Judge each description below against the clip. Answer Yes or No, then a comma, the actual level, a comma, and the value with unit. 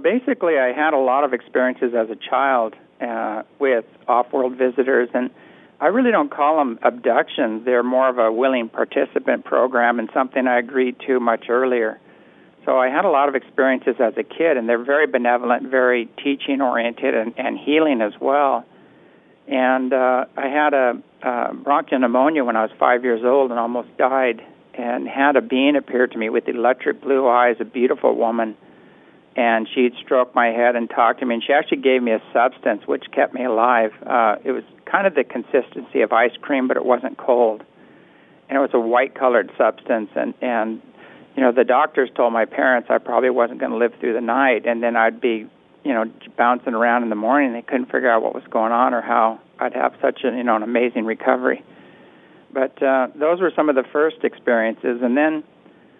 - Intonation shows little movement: Yes, narrow, 2.1 semitones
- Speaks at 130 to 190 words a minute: No, fast, 205 wpm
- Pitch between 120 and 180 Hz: Yes, low, 125 Hz